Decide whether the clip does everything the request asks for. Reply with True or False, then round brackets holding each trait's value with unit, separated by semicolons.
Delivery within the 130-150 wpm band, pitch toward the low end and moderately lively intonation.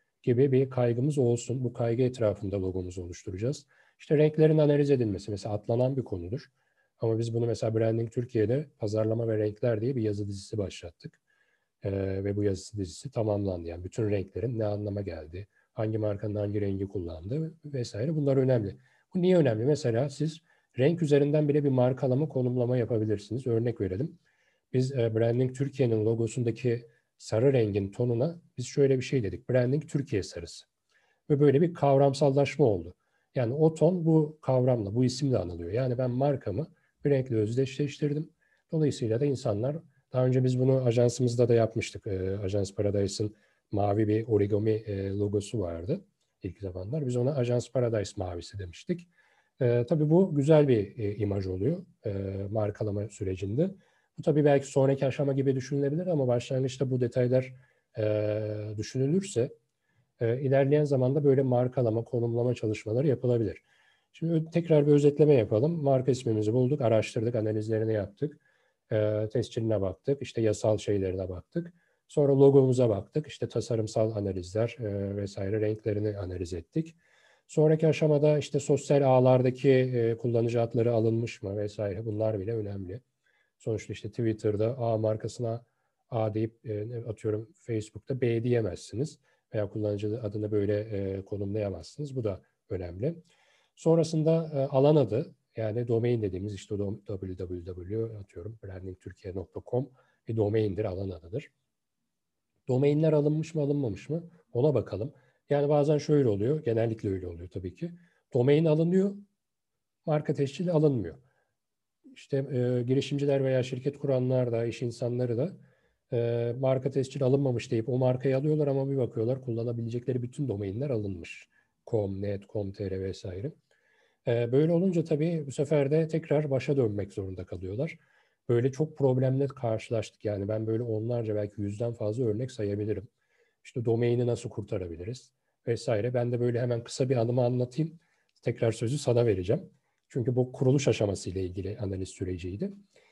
True (140 wpm; 120 Hz; 4.8 semitones)